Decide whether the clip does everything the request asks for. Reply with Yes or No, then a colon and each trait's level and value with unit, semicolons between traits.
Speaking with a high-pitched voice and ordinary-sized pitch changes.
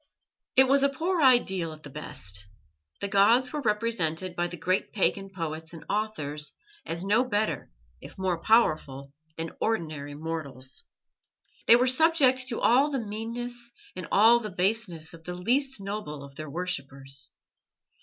No: high, 195 Hz; wide, 7.1 semitones